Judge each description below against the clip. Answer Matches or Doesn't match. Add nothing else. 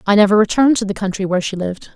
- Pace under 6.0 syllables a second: Doesn't match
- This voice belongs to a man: Doesn't match